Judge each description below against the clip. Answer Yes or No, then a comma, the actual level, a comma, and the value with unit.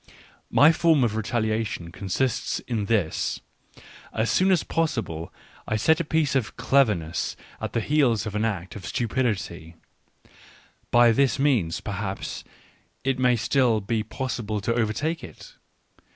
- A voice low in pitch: Yes, low, 115 Hz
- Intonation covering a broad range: No, average, 4.5 semitones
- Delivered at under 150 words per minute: Yes, slow, 135 wpm